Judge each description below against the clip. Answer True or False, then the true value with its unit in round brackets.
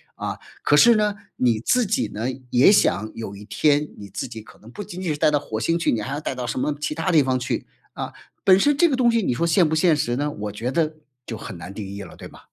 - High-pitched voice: False (145 Hz)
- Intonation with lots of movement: True (7.2 semitones)